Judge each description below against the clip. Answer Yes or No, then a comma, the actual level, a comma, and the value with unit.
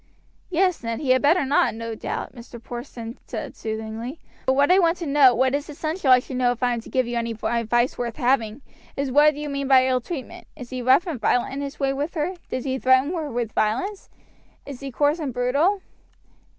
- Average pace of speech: No, fast, 230 wpm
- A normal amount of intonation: Yes, average, 3.5 semitones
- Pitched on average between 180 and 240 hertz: No, very high, 260 Hz